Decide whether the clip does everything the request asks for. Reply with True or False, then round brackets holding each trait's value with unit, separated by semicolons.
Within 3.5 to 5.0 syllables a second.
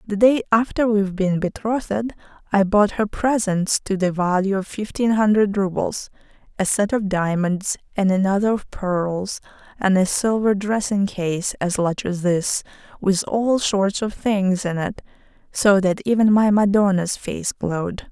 True (4.3 syllables/s)